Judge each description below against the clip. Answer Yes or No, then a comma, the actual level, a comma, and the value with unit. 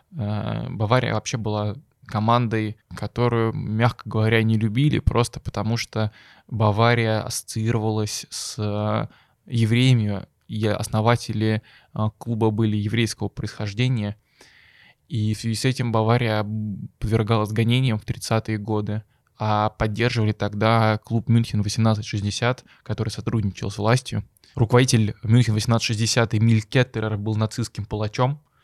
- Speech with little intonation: Yes, narrow, 1.7 semitones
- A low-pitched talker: Yes, low, 110 Hz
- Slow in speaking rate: Yes, slow, 105 wpm